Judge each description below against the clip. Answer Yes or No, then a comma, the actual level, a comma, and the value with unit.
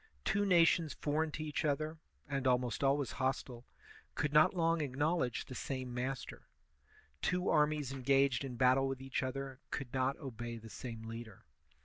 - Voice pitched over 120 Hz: Yes, low, 135 Hz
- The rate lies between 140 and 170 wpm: Yes, average, 155 wpm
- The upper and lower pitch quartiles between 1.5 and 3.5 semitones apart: Yes, average, 3.1 semitones